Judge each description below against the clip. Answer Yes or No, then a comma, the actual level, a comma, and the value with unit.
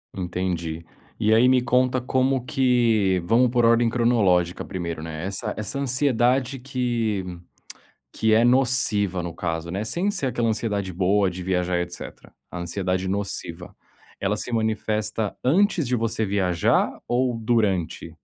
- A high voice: No, low, 110 Hz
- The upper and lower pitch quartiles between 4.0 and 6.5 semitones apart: Yes, average, 5.1 semitones